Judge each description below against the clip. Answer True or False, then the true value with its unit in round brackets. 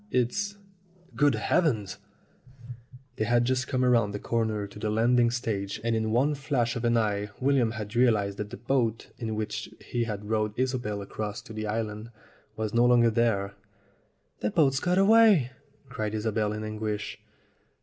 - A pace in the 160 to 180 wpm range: True (170 wpm)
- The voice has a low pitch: True (115 Hz)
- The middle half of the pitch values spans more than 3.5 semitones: False (2.8 semitones)